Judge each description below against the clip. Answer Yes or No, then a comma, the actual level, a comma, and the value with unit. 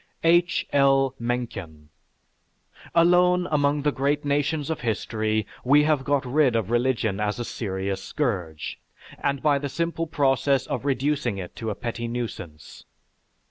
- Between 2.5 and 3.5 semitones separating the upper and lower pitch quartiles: No, average, 4.8 semitones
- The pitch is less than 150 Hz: Yes, low, 135 Hz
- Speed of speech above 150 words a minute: No, average, 140 wpm